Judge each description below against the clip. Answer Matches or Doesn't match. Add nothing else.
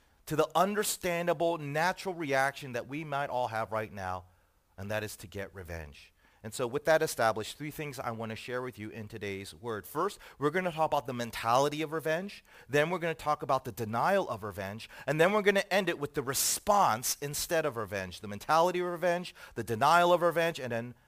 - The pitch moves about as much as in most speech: Doesn't match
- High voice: Doesn't match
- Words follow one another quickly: Matches